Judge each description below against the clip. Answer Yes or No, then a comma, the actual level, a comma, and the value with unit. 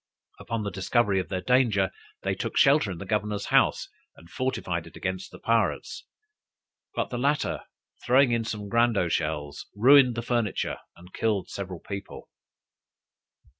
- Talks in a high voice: No, low, 105 Hz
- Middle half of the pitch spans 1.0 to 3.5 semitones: No, average, 4.2 semitones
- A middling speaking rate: Yes, average, 150 wpm